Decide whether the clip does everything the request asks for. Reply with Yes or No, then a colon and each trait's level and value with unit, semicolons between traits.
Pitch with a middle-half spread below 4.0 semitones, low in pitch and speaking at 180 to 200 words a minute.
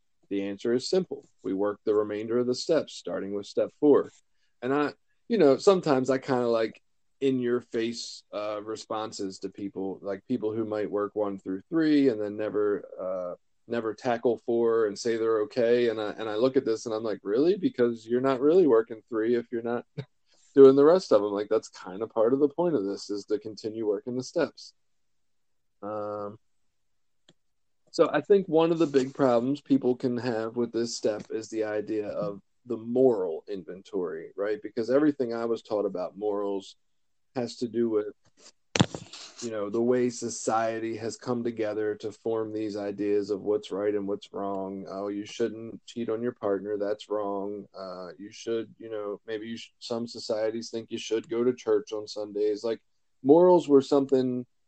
Yes: average, 3.3 semitones; low, 115 Hz; average, 190 wpm